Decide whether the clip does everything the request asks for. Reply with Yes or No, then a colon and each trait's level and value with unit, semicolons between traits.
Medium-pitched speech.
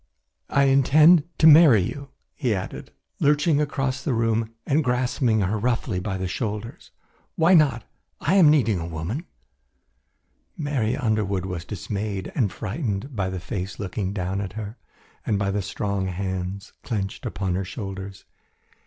No: low, 110 Hz